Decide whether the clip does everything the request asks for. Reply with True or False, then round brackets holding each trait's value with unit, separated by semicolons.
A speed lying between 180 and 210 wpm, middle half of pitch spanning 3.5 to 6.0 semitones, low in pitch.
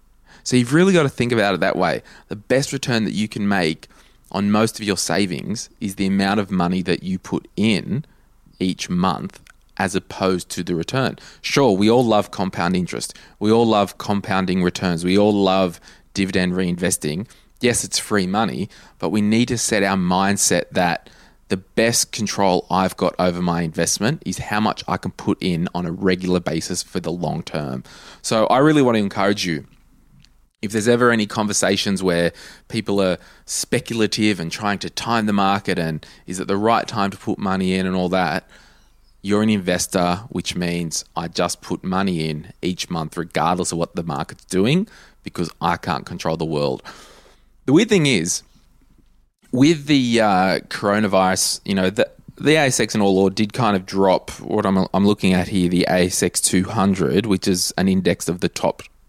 False (185 wpm; 2.9 semitones; 95 Hz)